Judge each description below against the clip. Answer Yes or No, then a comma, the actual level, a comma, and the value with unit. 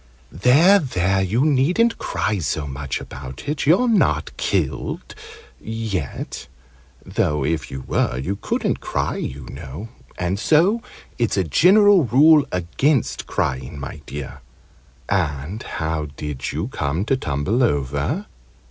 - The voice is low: Yes, very low, 95 Hz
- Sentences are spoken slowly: Yes, slow, 130 wpm